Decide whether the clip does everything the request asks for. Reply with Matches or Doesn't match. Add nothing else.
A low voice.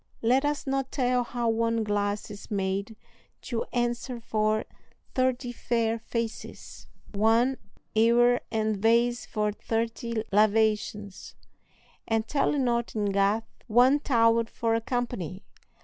Doesn't match